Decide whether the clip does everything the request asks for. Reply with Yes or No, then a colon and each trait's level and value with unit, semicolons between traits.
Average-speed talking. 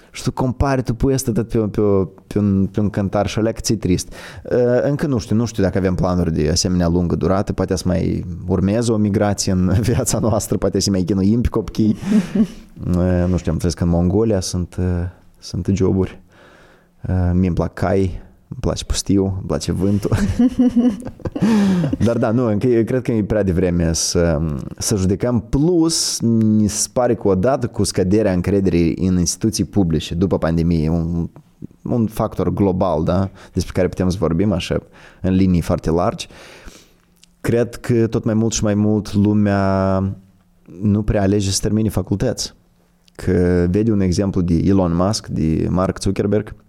Yes: average, 160 wpm